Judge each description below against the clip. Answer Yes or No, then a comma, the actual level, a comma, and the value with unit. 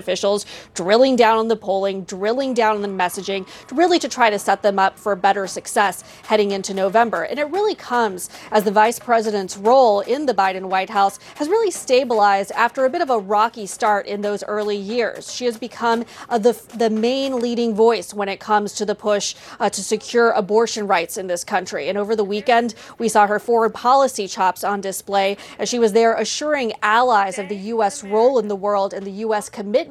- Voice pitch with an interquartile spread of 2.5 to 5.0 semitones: Yes, average, 2.8 semitones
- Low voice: No, high, 215 Hz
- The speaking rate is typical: No, fast, 210 wpm